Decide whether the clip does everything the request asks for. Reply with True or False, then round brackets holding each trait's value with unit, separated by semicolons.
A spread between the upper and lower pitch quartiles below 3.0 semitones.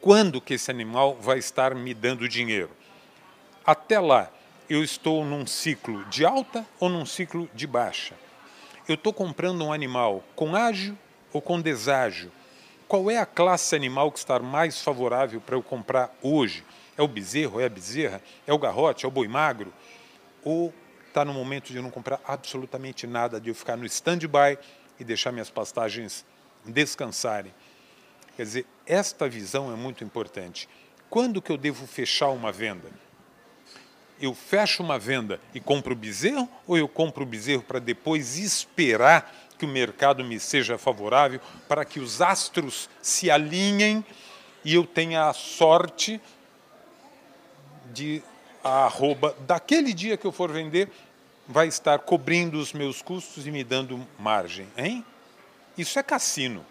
False (4.9 semitones)